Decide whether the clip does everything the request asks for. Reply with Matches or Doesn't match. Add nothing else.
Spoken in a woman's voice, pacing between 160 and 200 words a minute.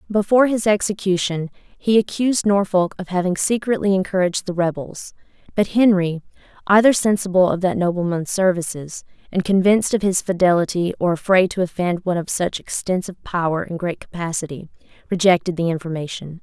Doesn't match